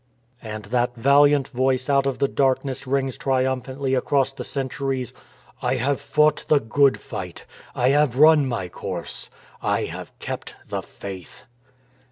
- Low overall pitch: Yes, low, 130 Hz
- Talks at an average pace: Yes, average, 150 wpm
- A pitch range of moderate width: No, narrow, 1.9 semitones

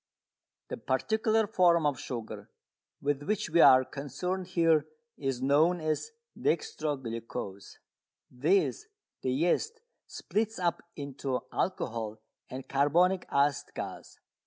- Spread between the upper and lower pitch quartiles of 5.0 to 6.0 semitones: Yes, wide, 5.5 semitones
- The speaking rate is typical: No, slow, 110 wpm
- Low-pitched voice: No, medium, 150 Hz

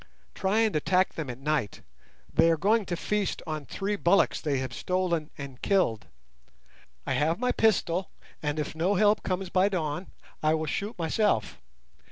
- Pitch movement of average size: Yes, average, 4.5 semitones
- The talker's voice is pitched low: No, medium, 170 Hz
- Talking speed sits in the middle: Yes, average, 170 wpm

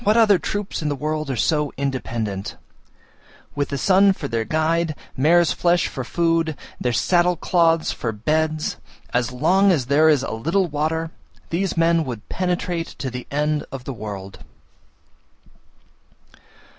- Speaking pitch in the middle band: Yes, medium, 155 Hz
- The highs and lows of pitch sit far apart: No, average, 4.6 semitones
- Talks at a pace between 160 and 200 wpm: No, average, 150 wpm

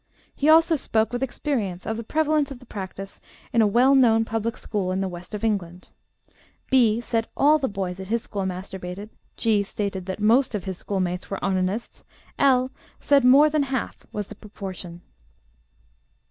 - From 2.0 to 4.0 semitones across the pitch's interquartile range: No, average, 5.0 semitones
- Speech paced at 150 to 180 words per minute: Yes, average, 175 wpm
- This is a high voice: Yes, high, 215 Hz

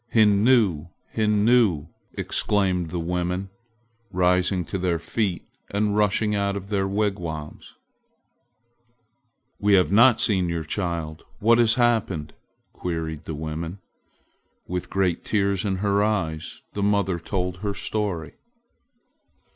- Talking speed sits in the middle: No, slow, 115 wpm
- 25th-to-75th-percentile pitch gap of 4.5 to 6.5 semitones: No, average, 3.3 semitones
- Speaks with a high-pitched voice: No, very low, 95 Hz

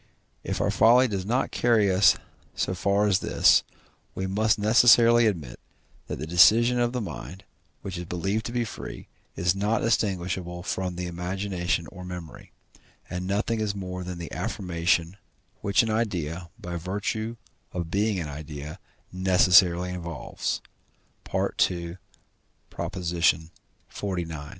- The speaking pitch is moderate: No, very low, 95 Hz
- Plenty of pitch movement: No, average, 3.4 semitones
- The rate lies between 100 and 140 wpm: Yes, slow, 135 wpm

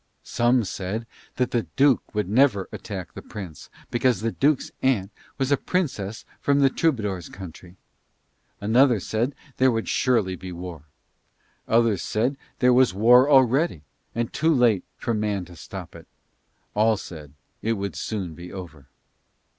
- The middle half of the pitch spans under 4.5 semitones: No, average, 5.3 semitones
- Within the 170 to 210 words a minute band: No, average, 155 wpm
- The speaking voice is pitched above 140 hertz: No, low, 110 Hz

